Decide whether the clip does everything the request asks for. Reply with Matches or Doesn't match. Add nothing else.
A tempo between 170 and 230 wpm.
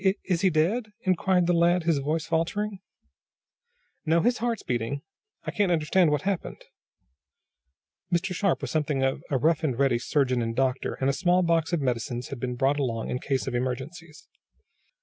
Matches